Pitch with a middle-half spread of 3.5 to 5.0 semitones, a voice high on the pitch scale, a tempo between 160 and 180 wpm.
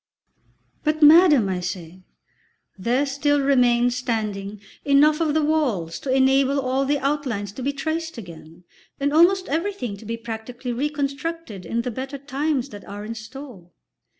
No: average, 4.7 semitones; very high, 265 Hz; average, 150 wpm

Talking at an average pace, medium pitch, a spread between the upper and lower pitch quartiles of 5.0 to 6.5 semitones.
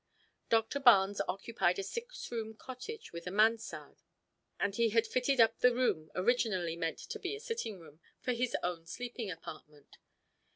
No: average, 165 wpm; high, 225 Hz; wide, 5.6 semitones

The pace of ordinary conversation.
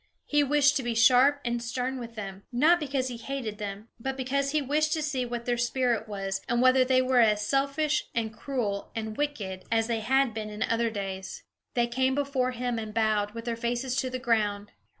No: fast, 210 wpm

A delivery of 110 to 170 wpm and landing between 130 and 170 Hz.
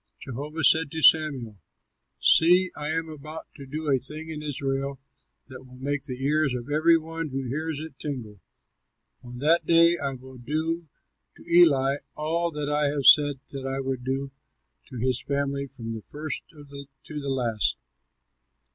Yes: average, 165 wpm; medium, 140 Hz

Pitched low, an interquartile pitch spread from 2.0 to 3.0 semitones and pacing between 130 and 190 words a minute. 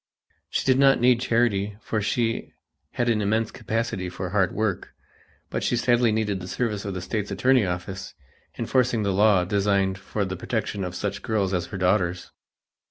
No: low, 105 Hz; average, 3.4 semitones; average, 175 wpm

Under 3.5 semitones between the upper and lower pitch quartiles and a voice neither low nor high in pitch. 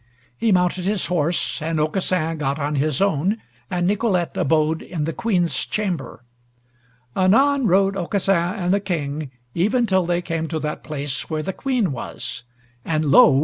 No: average, 4.0 semitones; medium, 175 Hz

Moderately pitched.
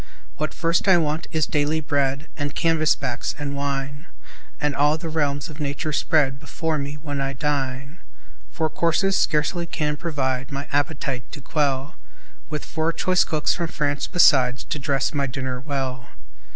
Yes: medium, 145 Hz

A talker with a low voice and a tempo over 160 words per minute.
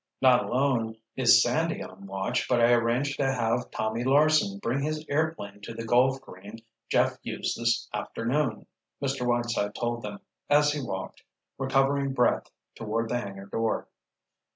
No: low, 120 Hz; average, 155 wpm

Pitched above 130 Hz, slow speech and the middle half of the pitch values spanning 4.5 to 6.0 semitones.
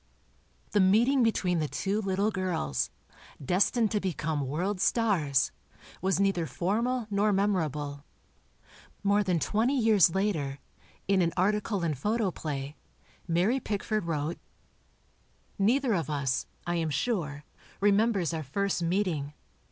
Yes: high, 190 Hz; slow, 120 wpm; average, 4.8 semitones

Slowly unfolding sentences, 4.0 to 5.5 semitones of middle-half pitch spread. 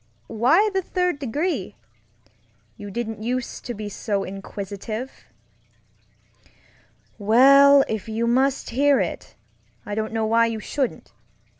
Yes: slow, 120 wpm; average, 4.3 semitones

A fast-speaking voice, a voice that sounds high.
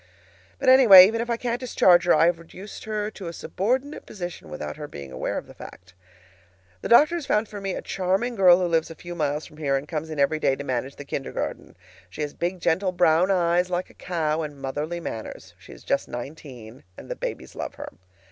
No: fast, 225 wpm; medium, 170 Hz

